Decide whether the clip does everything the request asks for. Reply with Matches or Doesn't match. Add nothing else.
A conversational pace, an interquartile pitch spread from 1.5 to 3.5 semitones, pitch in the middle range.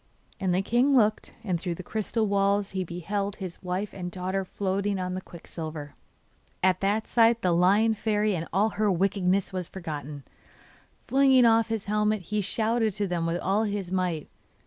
Doesn't match